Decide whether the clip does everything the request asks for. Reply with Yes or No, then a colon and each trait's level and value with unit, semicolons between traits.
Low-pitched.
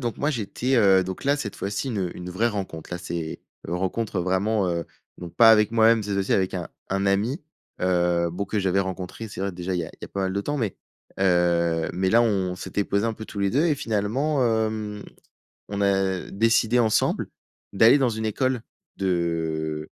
Yes: low, 100 Hz